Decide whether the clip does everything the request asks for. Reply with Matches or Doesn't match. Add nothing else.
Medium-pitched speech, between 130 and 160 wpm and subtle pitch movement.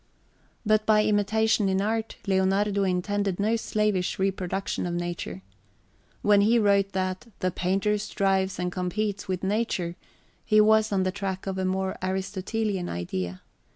Doesn't match